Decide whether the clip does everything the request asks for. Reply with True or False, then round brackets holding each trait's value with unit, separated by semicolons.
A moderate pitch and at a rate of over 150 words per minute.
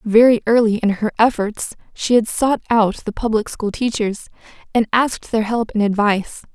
False (220 Hz; 175 wpm)